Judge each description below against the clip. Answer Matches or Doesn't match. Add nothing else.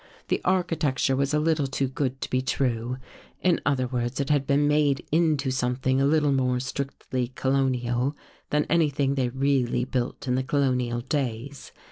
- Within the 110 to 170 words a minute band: Matches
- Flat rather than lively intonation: Matches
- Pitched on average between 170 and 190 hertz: Doesn't match